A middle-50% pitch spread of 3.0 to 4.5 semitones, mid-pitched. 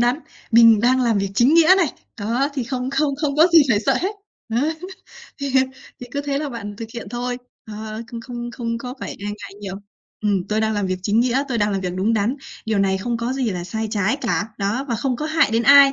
No: average, 4.1 semitones; high, 235 Hz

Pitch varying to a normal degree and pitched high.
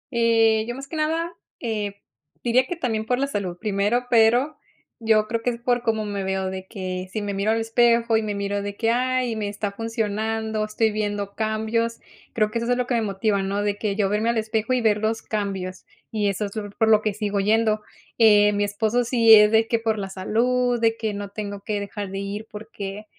No: narrow, 2.2 semitones; high, 220 Hz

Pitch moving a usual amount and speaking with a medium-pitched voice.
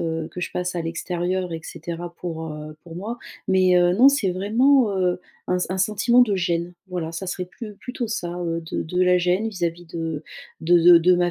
No: narrow, 2.1 semitones; medium, 180 Hz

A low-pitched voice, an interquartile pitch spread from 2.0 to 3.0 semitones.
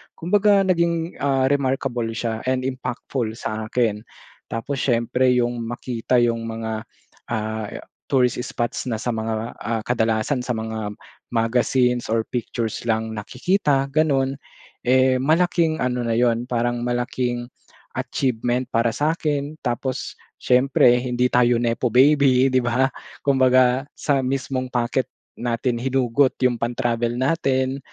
Yes: low, 125 Hz; narrow, 2.4 semitones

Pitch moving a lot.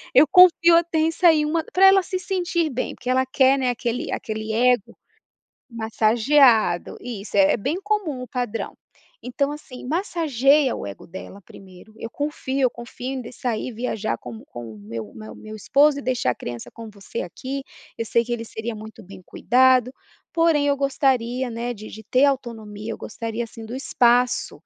No: average, 4.3 semitones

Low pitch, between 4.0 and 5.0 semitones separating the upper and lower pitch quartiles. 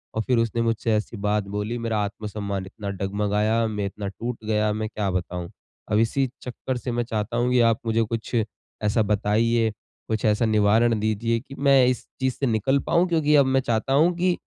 No: low, 110 Hz; average, 2.8 semitones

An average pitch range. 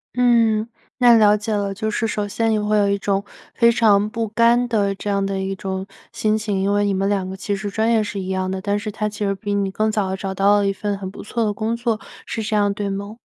No: narrow, 1.7 semitones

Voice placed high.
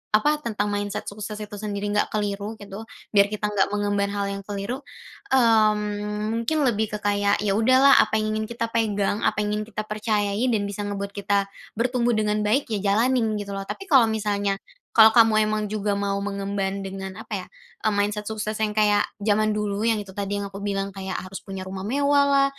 Yes: high, 210 Hz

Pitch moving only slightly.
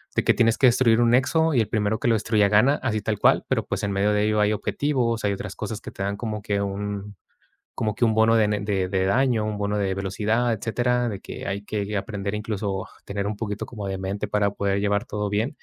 Yes: narrow, 2.1 semitones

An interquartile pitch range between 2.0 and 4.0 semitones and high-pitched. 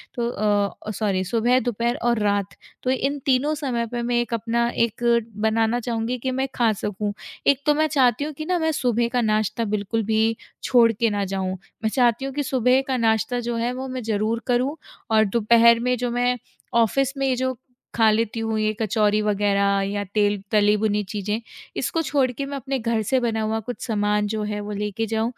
Yes: average, 2.8 semitones; high, 230 Hz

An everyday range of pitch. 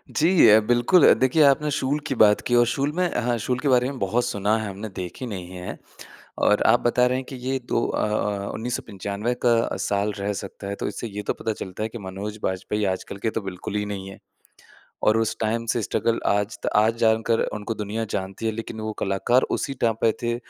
Yes: average, 3.0 semitones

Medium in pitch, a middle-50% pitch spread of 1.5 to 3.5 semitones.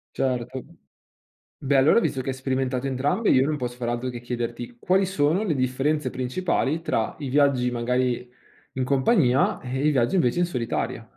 No: low, 130 Hz; average, 2.9 semitones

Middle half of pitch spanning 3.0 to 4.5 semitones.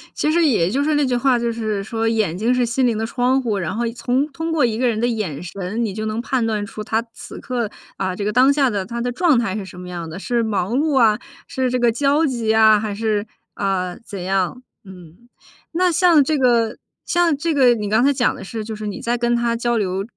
Yes: average, 3.6 semitones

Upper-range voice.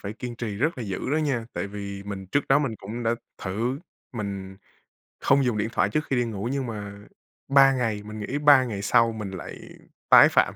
No: low, 115 Hz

